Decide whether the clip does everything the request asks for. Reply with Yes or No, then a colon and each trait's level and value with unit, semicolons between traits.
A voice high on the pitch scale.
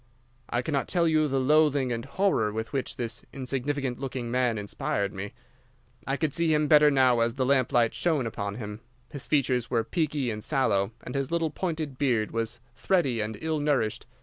No: low, 130 Hz